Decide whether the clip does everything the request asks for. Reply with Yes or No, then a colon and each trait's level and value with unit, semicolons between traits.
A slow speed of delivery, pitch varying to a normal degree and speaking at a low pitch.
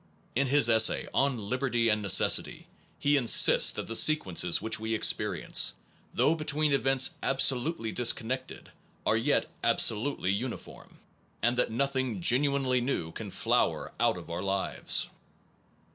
Yes: slow, 130 wpm; average, 3.8 semitones; low, 125 Hz